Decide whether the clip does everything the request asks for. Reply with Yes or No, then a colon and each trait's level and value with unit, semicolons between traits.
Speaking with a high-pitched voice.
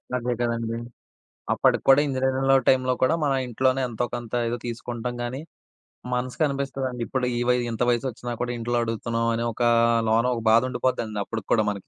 No: low, 120 Hz